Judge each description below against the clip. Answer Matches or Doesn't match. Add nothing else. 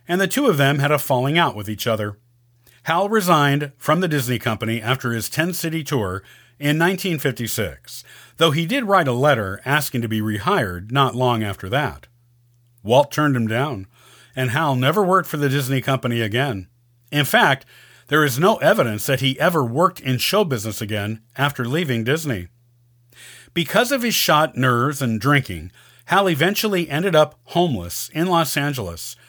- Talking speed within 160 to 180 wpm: Matches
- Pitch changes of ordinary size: Matches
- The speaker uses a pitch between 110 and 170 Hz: Matches